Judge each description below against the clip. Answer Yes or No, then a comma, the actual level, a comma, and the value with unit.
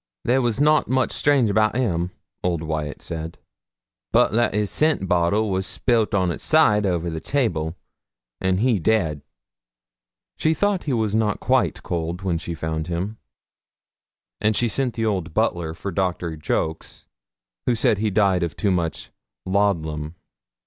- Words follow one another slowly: No, average, 160 wpm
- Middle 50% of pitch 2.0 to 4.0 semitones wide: No, average, 5.0 semitones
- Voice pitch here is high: No, very low, 95 Hz